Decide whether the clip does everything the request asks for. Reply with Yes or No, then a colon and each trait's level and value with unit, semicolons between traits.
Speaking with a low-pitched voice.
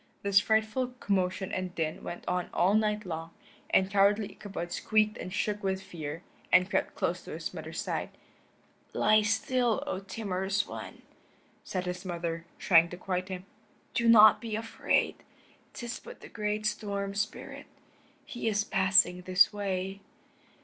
No: high, 195 Hz